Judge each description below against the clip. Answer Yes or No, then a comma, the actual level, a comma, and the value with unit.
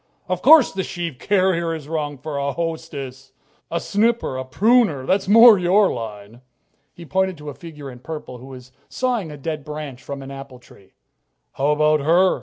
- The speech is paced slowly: No, average, 185 wpm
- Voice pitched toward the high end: No, medium, 155 Hz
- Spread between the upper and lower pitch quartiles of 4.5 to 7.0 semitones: Yes, average, 5.3 semitones